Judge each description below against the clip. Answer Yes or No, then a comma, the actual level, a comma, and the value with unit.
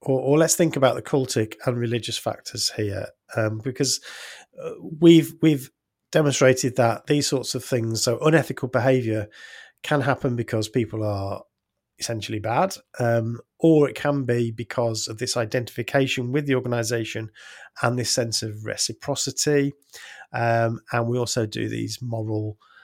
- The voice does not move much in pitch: No, average, 3.6 semitones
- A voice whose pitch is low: Yes, low, 125 Hz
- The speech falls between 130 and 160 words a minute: Yes, average, 145 wpm